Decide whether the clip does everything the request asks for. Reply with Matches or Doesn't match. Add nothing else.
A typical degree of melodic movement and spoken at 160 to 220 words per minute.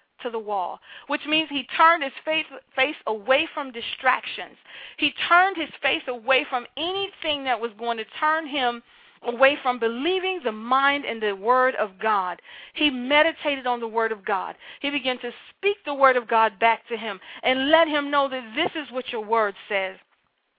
Matches